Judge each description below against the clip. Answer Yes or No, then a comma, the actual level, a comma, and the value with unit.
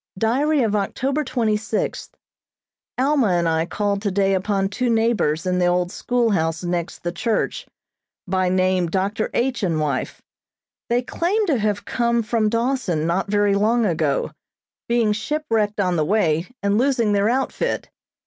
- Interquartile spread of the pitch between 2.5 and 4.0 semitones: No, average, 4.5 semitones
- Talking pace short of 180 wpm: Yes, average, 150 wpm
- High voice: Yes, high, 205 Hz